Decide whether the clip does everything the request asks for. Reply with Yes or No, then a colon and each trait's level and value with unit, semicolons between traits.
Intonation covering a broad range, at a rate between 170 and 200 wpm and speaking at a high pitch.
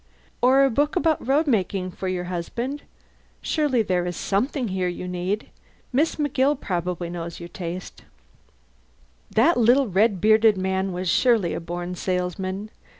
No: wide, 6.0 semitones; average, 150 wpm; high, 195 Hz